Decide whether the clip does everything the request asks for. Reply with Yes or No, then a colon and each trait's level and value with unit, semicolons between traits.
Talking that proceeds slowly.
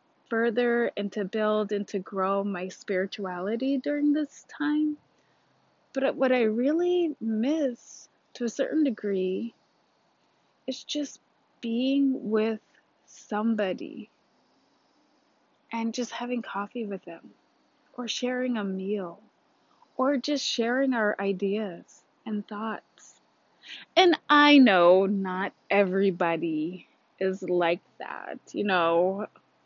Yes: slow, 105 wpm